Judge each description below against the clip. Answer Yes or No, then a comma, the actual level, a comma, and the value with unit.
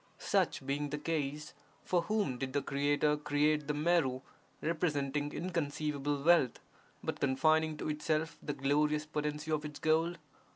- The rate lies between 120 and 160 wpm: Yes, average, 140 wpm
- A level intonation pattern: Yes, narrow, 1.6 semitones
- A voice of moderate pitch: Yes, medium, 150 Hz